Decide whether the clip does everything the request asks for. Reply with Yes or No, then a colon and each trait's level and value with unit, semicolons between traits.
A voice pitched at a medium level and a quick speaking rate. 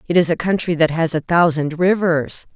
Yes: medium, 165 Hz; fast, 210 wpm